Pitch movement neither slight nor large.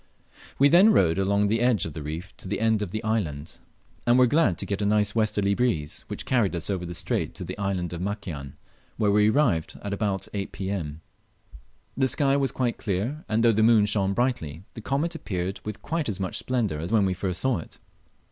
Yes: average, 4.3 semitones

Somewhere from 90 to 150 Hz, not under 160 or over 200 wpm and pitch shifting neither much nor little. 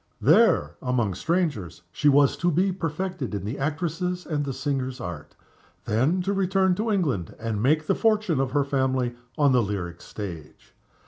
No: medium, 140 Hz; average, 170 wpm; wide, 6.9 semitones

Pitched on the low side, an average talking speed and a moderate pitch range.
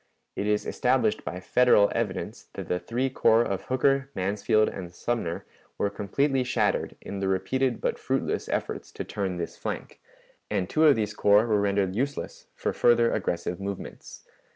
Yes: low, 105 Hz; average, 165 wpm; average, 4.3 semitones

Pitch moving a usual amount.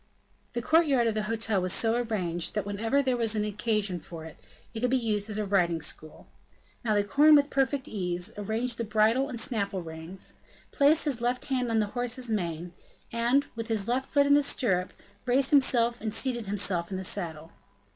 Yes: average, 4.2 semitones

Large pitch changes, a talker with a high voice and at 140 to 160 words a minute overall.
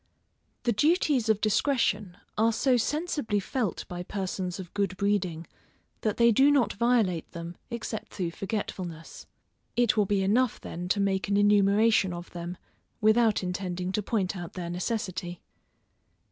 No: average, 4.0 semitones; high, 200 Hz; average, 150 wpm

